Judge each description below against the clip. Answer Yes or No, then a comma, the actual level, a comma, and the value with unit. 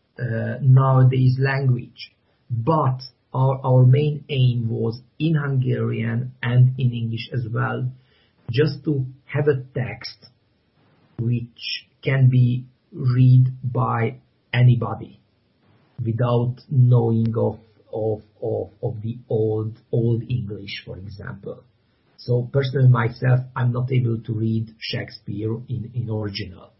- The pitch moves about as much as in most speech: No, narrow, 2.1 semitones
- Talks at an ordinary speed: No, slow, 115 wpm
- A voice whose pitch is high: No, low, 120 Hz